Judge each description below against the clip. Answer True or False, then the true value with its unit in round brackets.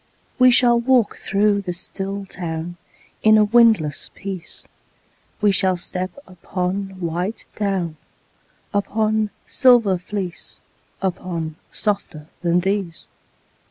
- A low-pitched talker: False (195 Hz)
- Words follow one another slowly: True (105 wpm)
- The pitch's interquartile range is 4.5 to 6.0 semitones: False (3.1 semitones)